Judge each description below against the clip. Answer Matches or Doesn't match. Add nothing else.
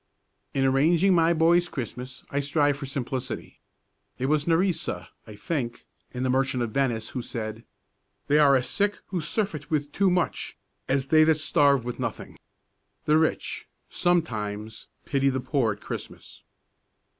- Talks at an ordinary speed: Matches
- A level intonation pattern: Doesn't match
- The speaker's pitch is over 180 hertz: Doesn't match